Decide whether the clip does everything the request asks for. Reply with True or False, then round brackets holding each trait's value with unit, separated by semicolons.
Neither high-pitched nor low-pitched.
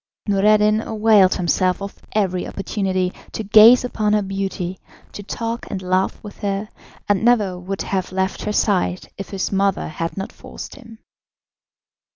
False (195 Hz)